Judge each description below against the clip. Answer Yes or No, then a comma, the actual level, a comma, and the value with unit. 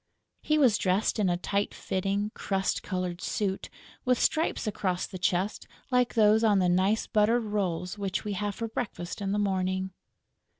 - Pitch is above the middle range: Yes, high, 200 Hz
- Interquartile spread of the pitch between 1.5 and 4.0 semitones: Yes, narrow, 2.4 semitones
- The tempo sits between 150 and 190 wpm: Yes, average, 170 wpm